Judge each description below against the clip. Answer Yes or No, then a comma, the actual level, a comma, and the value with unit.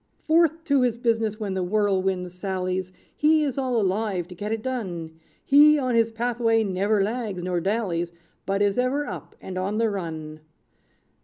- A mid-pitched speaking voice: No, high, 210 Hz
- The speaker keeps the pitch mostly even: No, average, 4.7 semitones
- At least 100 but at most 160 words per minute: No, average, 170 wpm